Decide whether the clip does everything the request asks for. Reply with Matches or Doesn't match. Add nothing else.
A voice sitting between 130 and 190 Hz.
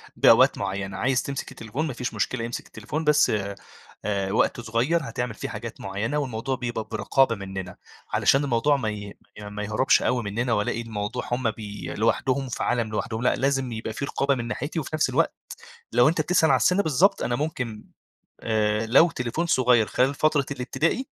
Doesn't match